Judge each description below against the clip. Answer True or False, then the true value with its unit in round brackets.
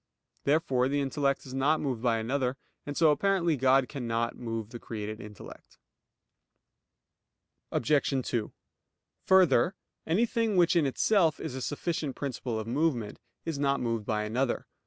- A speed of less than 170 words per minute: True (140 wpm)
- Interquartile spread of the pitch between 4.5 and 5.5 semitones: True (4.8 semitones)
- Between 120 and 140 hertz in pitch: True (135 Hz)